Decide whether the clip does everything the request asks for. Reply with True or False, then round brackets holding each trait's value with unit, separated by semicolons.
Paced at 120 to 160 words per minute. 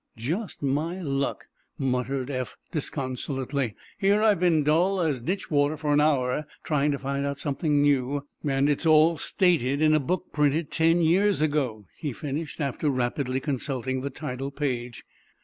True (155 wpm)